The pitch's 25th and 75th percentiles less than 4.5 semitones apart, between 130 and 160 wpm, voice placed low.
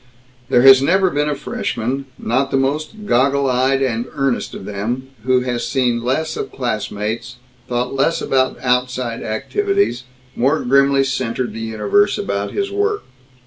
Yes: narrow, 2.5 semitones; average, 150 wpm; low, 130 Hz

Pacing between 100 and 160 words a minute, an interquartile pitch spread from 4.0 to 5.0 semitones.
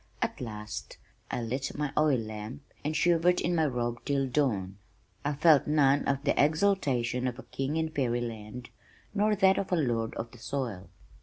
No: average, 175 wpm; average, 4.6 semitones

